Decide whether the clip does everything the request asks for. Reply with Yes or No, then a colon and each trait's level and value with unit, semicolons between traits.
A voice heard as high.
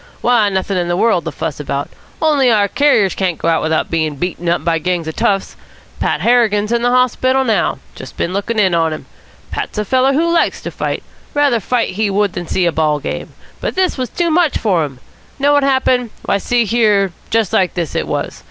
Yes: high, 205 Hz